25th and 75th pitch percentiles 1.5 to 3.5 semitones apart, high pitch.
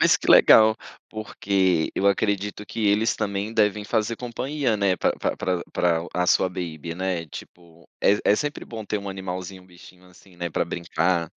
No: average, 3.1 semitones; very low, 95 Hz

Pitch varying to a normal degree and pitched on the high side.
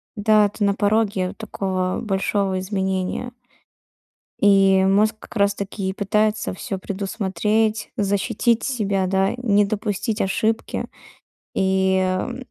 No: narrow, 2.1 semitones; high, 200 Hz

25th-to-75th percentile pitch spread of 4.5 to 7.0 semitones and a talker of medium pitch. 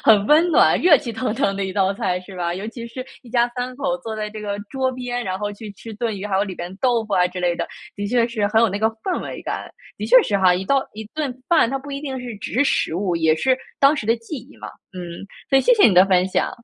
No: average, 4.8 semitones; high, 220 Hz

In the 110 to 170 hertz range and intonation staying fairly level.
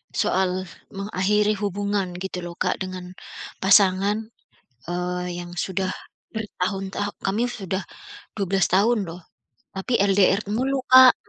No: high, 195 Hz; narrow, 2.1 semitones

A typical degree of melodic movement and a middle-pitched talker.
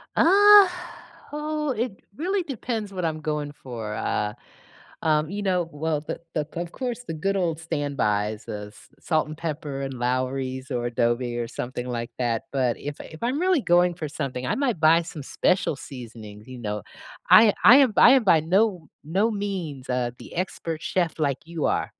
No: wide, 7.6 semitones; medium, 155 Hz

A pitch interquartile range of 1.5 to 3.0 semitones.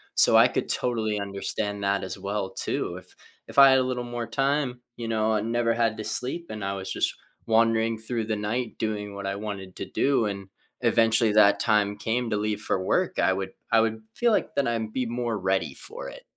Yes: narrow, 2.6 semitones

